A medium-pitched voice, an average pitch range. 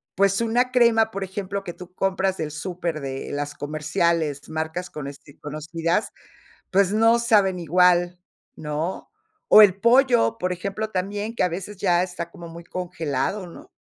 Yes: medium, 180 Hz; average, 3.8 semitones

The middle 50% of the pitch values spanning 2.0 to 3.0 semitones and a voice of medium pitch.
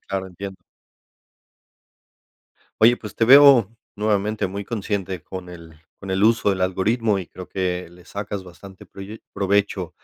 No: narrow, 2.4 semitones; very low, 95 Hz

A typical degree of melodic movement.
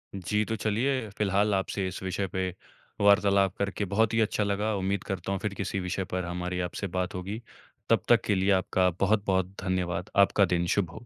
No: narrow, 1.9 semitones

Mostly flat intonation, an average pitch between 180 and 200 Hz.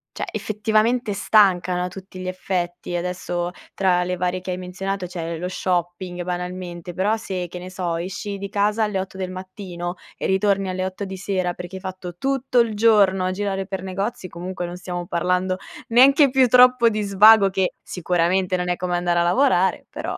Yes: narrow, 2.1 semitones; medium, 185 Hz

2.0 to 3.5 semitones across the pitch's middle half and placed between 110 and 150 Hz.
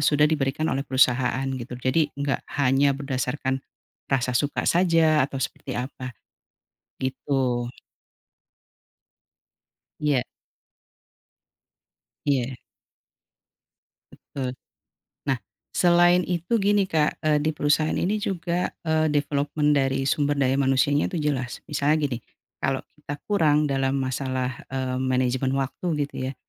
Yes: narrow, 2.6 semitones; medium, 140 Hz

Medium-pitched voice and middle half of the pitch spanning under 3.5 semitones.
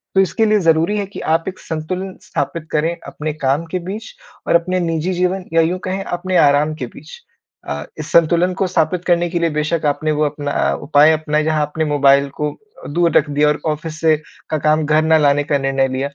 Yes: medium, 160 Hz; average, 2.9 semitones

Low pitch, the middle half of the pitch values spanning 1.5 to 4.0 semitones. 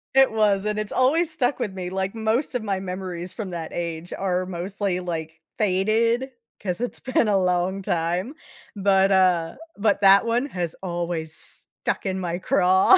No: high, 190 Hz; average, 3.4 semitones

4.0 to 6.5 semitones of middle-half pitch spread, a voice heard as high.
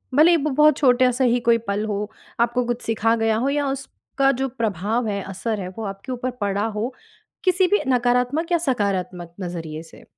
Yes: average, 4.7 semitones; high, 235 Hz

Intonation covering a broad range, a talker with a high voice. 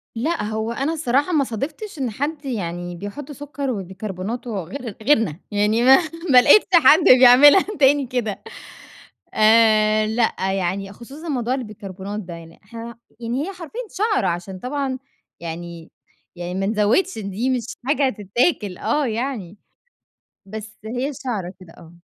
Yes: wide, 5.7 semitones; high, 230 Hz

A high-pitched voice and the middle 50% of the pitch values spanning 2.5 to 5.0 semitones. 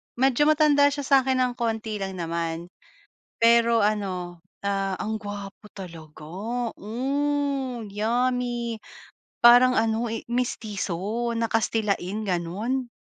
Yes: high, 225 Hz; average, 4.0 semitones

